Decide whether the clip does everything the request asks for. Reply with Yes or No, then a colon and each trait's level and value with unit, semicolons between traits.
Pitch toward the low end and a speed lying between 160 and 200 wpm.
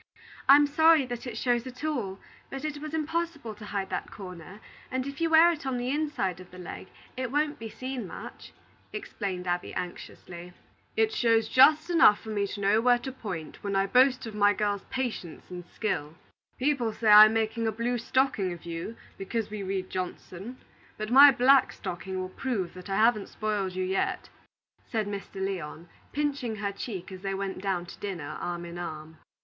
No: high, 215 Hz; average, 190 wpm